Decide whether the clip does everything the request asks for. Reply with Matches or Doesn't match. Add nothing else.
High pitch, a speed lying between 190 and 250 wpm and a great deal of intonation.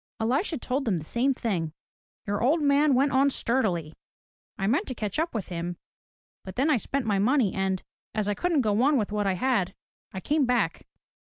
Matches